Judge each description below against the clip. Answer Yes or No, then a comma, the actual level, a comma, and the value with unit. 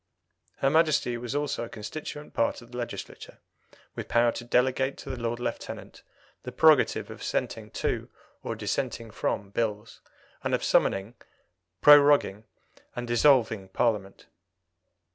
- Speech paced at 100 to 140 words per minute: Yes, slow, 135 wpm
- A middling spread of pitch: Yes, average, 3.5 semitones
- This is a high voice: No, low, 120 Hz